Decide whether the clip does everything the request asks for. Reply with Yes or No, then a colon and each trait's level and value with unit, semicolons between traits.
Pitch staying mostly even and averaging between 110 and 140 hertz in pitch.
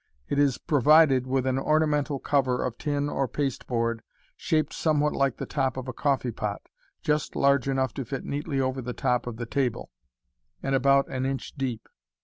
Yes: narrow, 2.2 semitones; low, 135 Hz